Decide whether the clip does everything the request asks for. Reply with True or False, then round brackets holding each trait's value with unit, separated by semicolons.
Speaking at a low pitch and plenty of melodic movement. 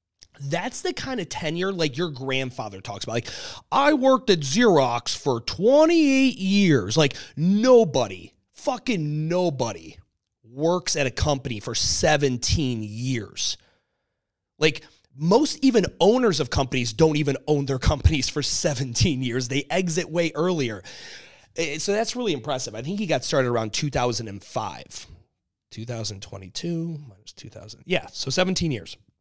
False (145 Hz; 7.3 semitones)